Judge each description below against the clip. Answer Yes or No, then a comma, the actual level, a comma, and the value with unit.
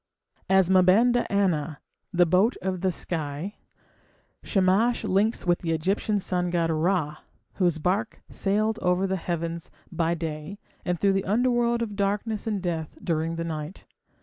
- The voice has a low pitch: No, medium, 185 Hz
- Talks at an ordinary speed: Yes, average, 150 wpm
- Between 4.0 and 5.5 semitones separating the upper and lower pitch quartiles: No, average, 3.4 semitones